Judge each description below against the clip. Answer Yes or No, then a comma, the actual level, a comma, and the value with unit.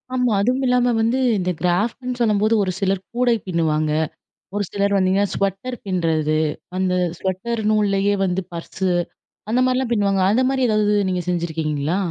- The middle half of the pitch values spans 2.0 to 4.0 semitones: No, average, 4.5 semitones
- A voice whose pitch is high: Yes, high, 195 Hz